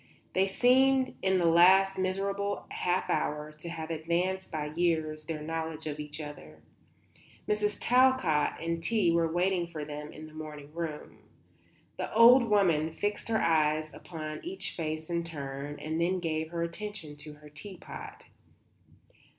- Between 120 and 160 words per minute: Yes, average, 155 wpm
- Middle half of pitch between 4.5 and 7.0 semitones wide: No, average, 3.7 semitones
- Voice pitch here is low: No, medium, 165 Hz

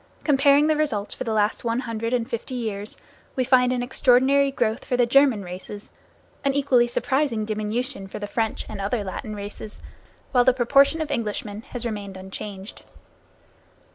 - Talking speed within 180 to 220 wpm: No, average, 170 wpm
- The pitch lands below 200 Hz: No, high, 235 Hz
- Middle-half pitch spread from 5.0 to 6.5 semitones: No, average, 4.0 semitones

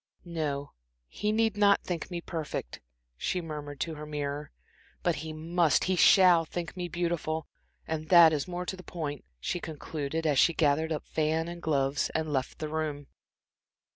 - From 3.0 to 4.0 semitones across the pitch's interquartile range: No, narrow, 2.6 semitones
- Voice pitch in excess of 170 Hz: No, medium, 160 Hz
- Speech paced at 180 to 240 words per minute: No, average, 170 wpm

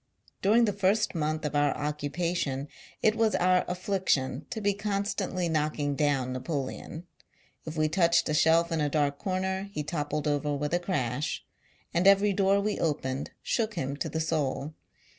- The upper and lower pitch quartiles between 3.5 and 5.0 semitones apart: Yes, average, 4.7 semitones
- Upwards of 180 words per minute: No, average, 175 wpm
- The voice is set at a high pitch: No, medium, 160 Hz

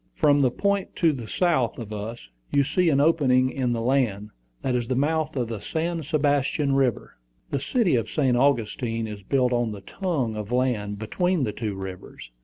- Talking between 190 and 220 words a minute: Yes, average, 195 wpm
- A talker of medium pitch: No, low, 130 Hz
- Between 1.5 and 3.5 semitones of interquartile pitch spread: No, average, 4.8 semitones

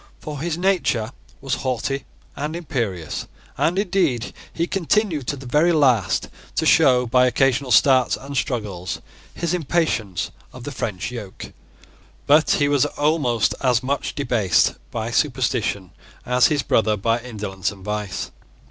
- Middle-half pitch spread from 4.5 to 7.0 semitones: Yes, average, 5.0 semitones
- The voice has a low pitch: Yes, low, 130 Hz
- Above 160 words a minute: No, average, 140 wpm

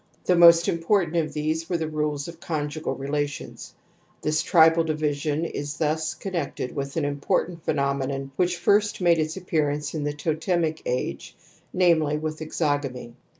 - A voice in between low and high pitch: Yes, medium, 155 Hz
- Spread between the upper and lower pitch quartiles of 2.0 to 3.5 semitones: Yes, narrow, 2.5 semitones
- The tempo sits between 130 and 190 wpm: Yes, average, 155 wpm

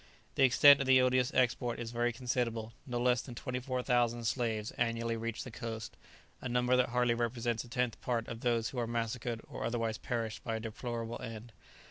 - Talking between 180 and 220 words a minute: Yes, average, 190 wpm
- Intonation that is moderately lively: No, narrow, 1.4 semitones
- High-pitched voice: No, low, 120 Hz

